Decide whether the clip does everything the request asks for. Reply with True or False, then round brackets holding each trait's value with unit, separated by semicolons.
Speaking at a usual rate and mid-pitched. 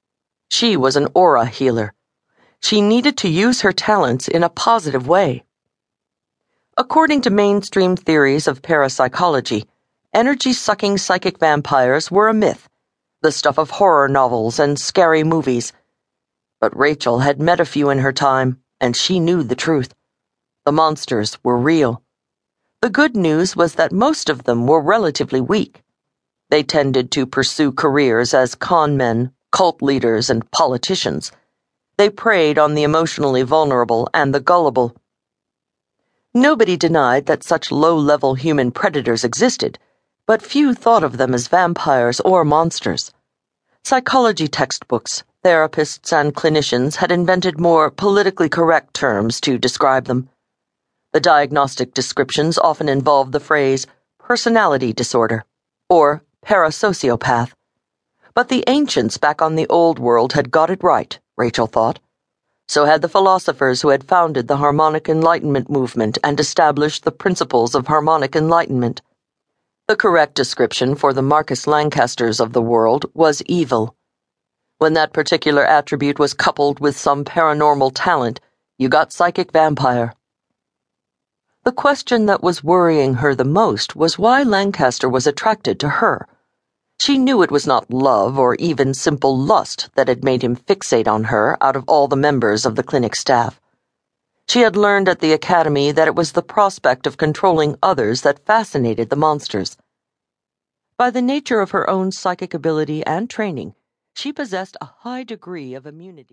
True (150 wpm; 150 Hz)